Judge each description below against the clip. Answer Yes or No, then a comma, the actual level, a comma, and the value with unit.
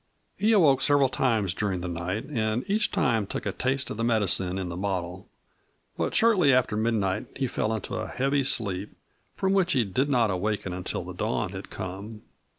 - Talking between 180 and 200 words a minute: Yes, average, 190 wpm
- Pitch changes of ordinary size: No, wide, 5.9 semitones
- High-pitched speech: No, low, 110 Hz